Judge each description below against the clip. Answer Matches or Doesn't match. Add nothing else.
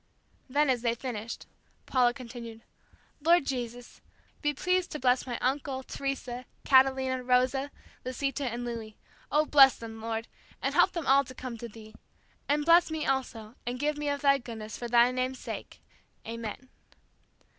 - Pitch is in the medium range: Doesn't match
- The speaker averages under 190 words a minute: Matches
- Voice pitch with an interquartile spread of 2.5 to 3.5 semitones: Matches